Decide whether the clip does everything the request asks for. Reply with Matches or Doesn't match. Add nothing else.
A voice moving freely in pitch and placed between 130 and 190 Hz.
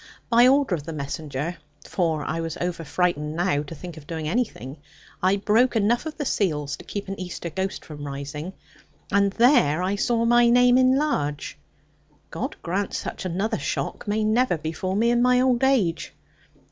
Matches